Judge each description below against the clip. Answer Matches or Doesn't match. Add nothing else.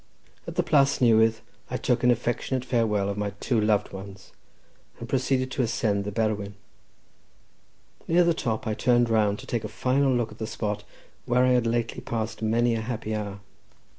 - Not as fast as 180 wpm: Doesn't match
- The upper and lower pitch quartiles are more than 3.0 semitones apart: Doesn't match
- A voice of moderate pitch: Doesn't match